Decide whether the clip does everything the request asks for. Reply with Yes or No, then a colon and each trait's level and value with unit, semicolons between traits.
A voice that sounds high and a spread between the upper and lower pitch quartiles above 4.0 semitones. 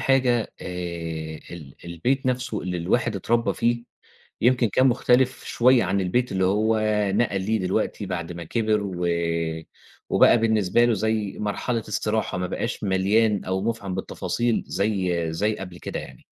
No: low, 105 Hz; average, 4.4 semitones